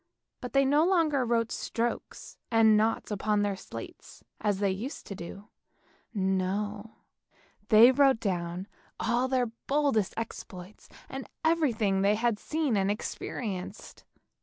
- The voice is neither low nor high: No, high, 220 Hz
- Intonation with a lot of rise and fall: No, average, 4.4 semitones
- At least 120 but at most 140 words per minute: Yes, slow, 135 wpm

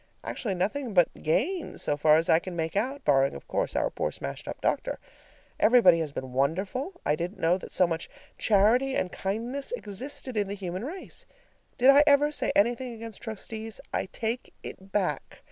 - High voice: Yes, high, 205 Hz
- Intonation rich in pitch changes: Yes, wide, 6.6 semitones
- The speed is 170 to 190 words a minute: Yes, average, 185 wpm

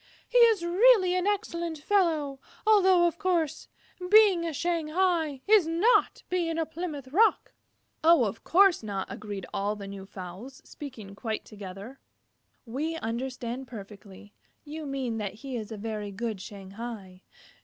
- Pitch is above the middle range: Yes, very high, 275 Hz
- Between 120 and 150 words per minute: Yes, average, 140 wpm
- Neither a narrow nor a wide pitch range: No, wide, 8.4 semitones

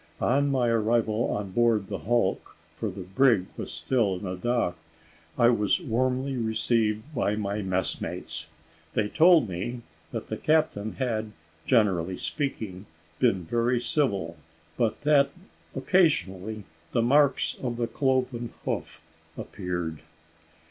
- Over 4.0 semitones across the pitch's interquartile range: Yes, average, 4.5 semitones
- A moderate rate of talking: No, slow, 125 wpm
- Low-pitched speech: Yes, low, 115 Hz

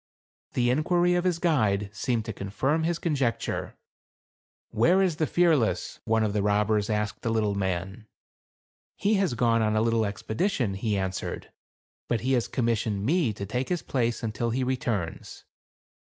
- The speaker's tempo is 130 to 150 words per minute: No, average, 175 wpm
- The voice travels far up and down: Yes, wide, 5.7 semitones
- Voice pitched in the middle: No, low, 115 Hz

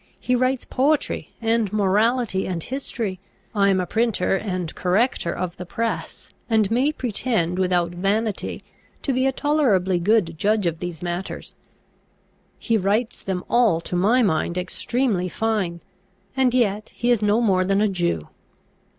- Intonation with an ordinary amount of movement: Yes, average, 4.6 semitones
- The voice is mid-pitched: No, high, 205 Hz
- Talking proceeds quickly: No, average, 150 wpm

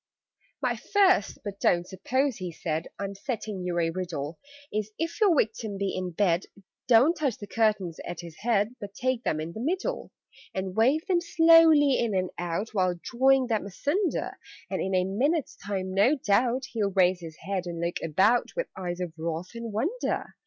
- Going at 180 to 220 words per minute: Yes, average, 185 wpm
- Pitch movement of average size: No, wide, 6.2 semitones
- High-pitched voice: Yes, high, 205 Hz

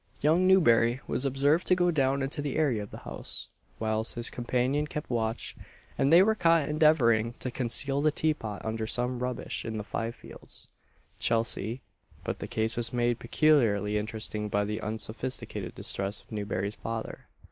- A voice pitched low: Yes, low, 120 Hz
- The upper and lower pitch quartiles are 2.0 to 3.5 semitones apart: No, average, 4.5 semitones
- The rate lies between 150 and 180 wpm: Yes, average, 170 wpm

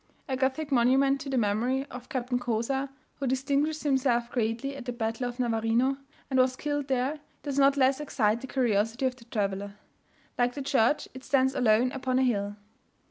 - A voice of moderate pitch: No, very high, 255 Hz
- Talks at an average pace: Yes, average, 185 wpm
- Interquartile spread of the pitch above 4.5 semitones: No, narrow, 2.5 semitones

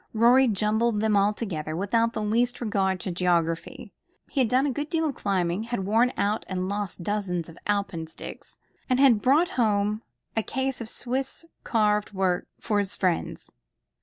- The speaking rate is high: No, average, 170 wpm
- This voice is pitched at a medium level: No, high, 210 Hz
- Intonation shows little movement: No, average, 4.0 semitones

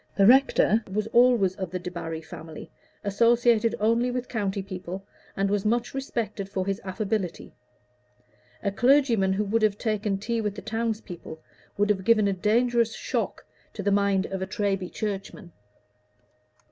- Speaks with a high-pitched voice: Yes, high, 205 Hz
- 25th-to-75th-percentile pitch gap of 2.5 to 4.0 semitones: Yes, average, 3.0 semitones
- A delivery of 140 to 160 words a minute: Yes, average, 155 wpm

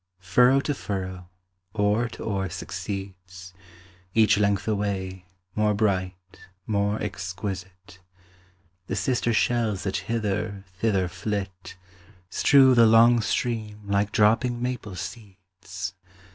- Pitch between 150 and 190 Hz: No, low, 100 Hz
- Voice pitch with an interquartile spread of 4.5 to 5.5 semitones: No, average, 2.8 semitones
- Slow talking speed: Yes, slow, 105 wpm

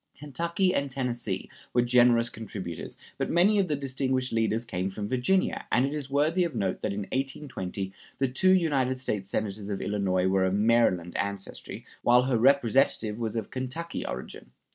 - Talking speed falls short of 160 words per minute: No, average, 170 wpm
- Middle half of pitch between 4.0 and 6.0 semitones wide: Yes, average, 5.3 semitones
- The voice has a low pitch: Yes, low, 120 Hz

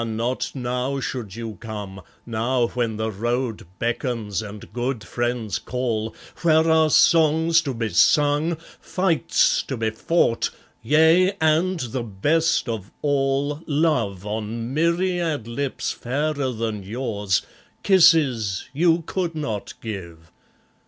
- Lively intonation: Yes, wide, 5.9 semitones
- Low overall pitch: Yes, low, 125 Hz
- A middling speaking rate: No, slow, 120 wpm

